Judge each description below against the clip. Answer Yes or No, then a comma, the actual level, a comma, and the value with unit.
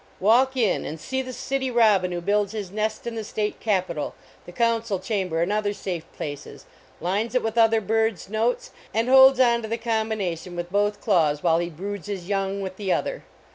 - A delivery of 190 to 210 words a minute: Yes, average, 200 wpm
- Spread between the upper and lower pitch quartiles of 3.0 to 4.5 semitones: Yes, average, 3.7 semitones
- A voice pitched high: Yes, high, 210 Hz